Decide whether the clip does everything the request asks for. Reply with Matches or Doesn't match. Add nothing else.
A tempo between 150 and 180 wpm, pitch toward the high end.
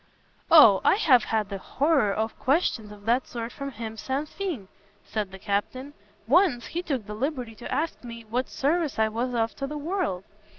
Doesn't match